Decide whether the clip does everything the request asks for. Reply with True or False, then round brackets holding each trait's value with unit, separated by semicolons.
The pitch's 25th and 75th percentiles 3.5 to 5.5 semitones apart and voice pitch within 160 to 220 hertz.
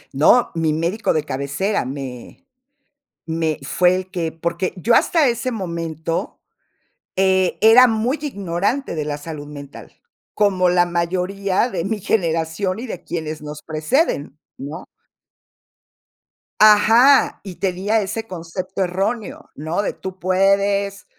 True (4.1 semitones; 185 Hz)